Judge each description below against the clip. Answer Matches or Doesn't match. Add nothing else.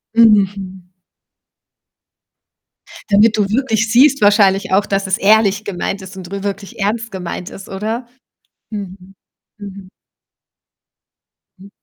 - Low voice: Doesn't match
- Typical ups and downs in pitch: Doesn't match